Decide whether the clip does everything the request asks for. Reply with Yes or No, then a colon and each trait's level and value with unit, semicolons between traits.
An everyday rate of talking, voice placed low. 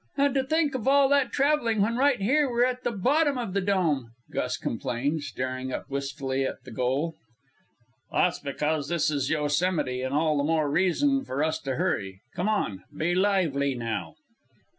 No: average, 180 wpm; medium, 160 Hz